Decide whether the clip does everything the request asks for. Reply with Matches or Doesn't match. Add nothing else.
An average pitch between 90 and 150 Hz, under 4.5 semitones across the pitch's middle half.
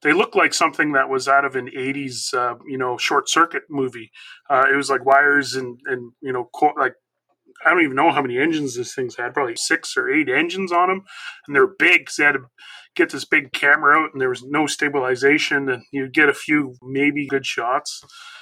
Doesn't match